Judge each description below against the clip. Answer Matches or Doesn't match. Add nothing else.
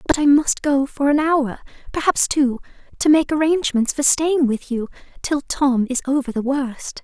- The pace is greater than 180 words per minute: Matches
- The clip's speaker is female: Matches